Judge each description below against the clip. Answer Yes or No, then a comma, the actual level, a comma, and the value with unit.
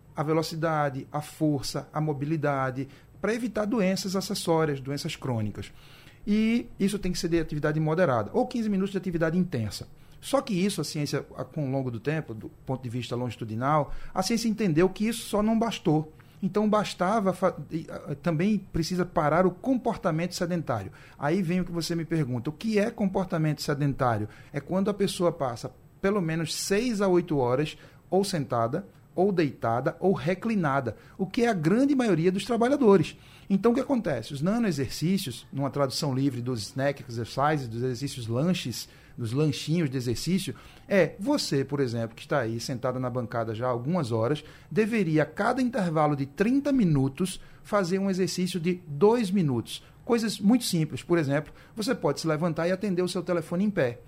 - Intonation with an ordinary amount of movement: No, wide, 5.7 semitones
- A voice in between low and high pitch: Yes, medium, 160 Hz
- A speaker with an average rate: Yes, average, 175 wpm